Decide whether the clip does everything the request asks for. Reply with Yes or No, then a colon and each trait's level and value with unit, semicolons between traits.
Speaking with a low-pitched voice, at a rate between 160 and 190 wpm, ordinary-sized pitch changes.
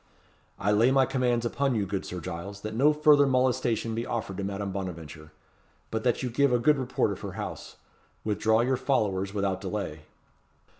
Yes: low, 110 Hz; average, 185 wpm; average, 4.7 semitones